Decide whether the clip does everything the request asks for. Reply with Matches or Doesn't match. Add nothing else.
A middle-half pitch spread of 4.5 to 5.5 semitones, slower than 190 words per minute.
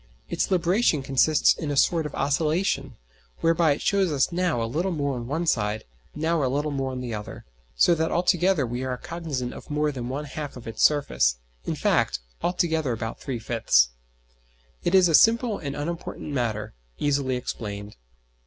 Matches